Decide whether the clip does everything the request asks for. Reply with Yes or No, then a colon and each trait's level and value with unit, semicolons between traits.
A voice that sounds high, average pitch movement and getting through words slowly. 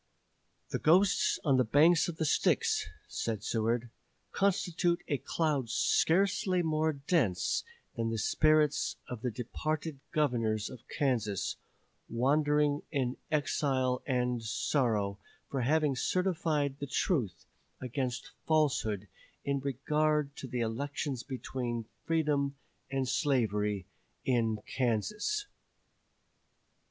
No: low, 135 Hz; average, 4.5 semitones; slow, 105 wpm